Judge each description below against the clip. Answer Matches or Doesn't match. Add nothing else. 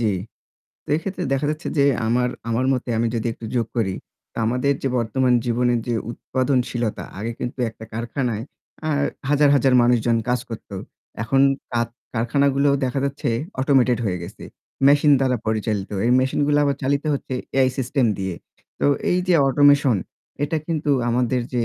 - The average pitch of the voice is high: Doesn't match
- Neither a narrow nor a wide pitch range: Matches